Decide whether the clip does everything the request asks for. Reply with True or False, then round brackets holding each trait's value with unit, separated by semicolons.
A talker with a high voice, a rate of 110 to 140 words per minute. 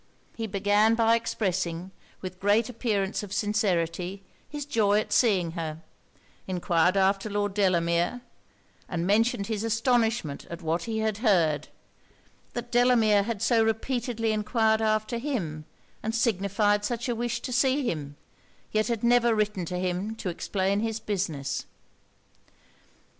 True (210 Hz; 135 wpm)